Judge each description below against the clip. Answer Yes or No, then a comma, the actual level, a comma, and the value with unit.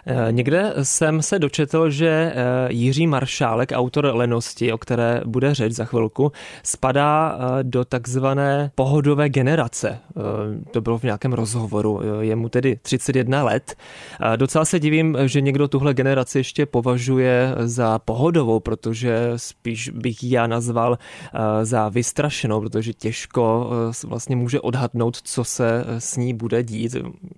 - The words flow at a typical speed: Yes, average, 130 wpm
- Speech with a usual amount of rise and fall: Yes, average, 3.3 semitones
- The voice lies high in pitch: No, low, 125 Hz